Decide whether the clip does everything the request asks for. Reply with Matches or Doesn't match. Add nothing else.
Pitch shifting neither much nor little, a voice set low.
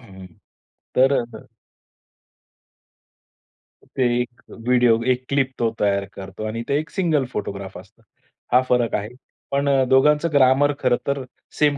Matches